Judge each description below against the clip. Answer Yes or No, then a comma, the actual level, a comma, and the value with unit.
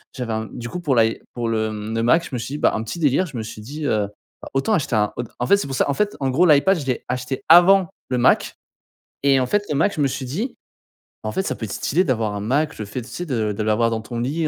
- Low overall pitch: Yes, low, 130 Hz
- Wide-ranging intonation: Yes, wide, 5.7 semitones